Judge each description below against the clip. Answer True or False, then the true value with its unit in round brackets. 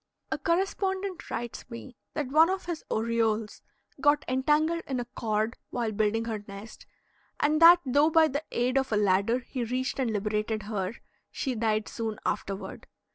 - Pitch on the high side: True (240 Hz)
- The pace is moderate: True (165 wpm)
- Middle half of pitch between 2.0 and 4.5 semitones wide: False (5.4 semitones)